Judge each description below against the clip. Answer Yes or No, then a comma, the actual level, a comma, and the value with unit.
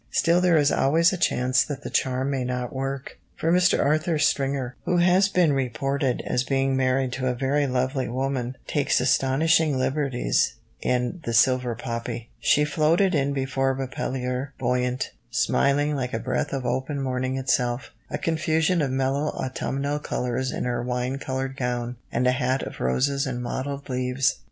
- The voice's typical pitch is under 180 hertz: Yes, low, 135 Hz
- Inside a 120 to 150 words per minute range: No, average, 165 wpm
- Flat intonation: Yes, narrow, 2.2 semitones